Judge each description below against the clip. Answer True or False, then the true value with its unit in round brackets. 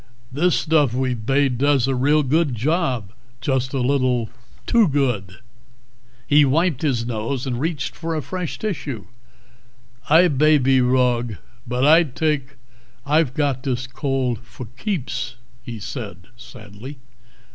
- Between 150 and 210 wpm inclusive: False (135 wpm)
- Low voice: True (130 Hz)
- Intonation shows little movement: False (3.5 semitones)